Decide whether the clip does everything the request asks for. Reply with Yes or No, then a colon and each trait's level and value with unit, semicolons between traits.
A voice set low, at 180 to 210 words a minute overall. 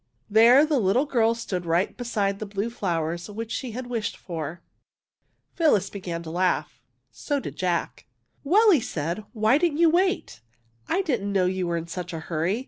No: high, 205 Hz; average, 190 wpm